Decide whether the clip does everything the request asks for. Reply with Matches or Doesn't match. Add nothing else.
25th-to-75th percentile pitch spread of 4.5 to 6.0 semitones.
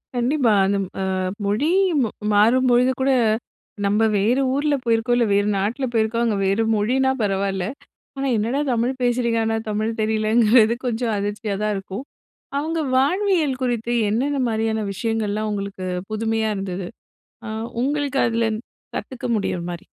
Doesn't match